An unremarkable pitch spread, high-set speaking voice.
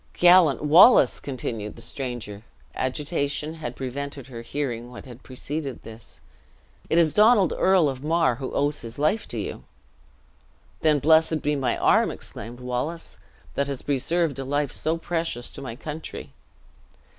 No: average, 4.2 semitones; medium, 140 Hz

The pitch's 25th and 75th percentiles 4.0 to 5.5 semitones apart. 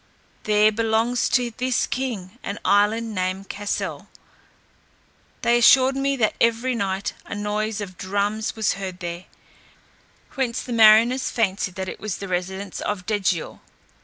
No: average, 3.3 semitones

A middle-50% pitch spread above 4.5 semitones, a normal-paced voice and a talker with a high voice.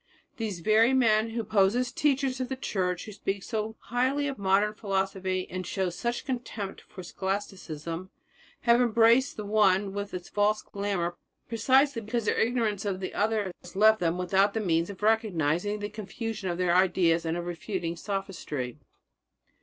No: average, 3.4 semitones; average, 170 wpm; high, 205 Hz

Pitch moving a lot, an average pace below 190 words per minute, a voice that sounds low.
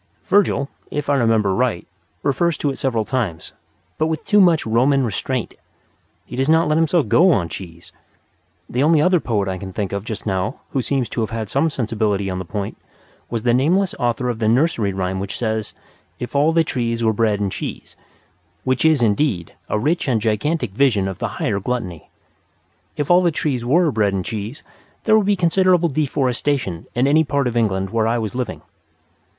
No: wide, 5.9 semitones; average, 195 wpm; low, 120 Hz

